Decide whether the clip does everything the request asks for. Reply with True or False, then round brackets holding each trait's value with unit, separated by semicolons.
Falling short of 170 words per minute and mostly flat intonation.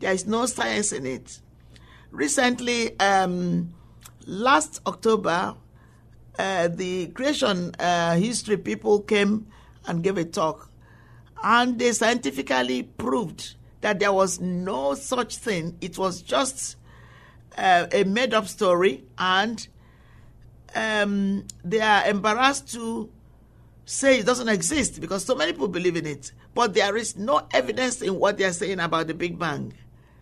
False (140 wpm; 4.7 semitones)